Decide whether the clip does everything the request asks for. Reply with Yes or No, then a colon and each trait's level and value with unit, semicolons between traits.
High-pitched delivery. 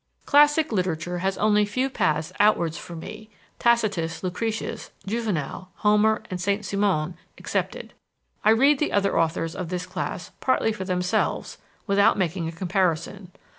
Yes: high, 195 Hz